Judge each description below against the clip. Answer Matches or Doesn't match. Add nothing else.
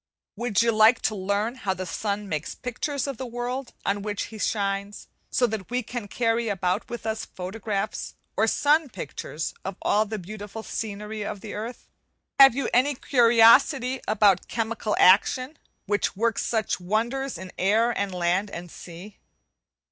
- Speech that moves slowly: Doesn't match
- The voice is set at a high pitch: Matches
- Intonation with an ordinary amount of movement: Matches